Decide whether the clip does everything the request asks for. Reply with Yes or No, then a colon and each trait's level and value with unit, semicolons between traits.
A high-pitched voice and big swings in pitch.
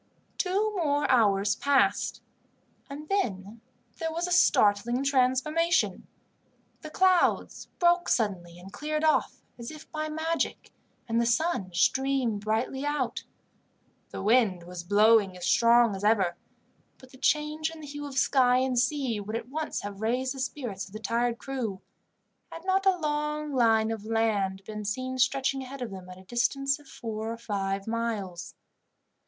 Yes: high, 245 Hz; wide, 5.9 semitones